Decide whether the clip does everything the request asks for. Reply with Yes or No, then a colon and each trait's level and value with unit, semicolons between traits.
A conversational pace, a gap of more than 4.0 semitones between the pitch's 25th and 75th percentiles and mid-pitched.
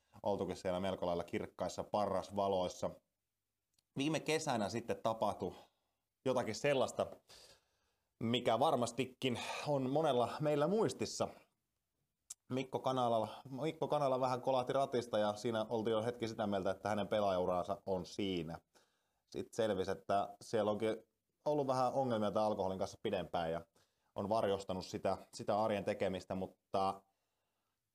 No: average, 120 wpm; average, 4.7 semitones; low, 110 Hz